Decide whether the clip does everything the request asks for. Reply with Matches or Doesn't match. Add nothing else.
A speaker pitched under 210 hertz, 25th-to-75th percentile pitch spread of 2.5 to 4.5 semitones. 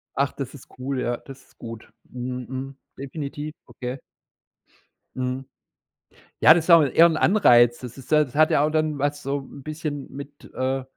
Matches